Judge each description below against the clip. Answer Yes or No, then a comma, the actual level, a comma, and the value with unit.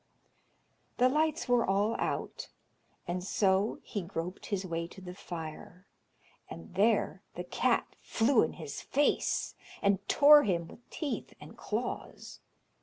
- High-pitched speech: Yes, high, 195 Hz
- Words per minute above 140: No, slow, 135 wpm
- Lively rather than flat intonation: Yes, wide, 5.7 semitones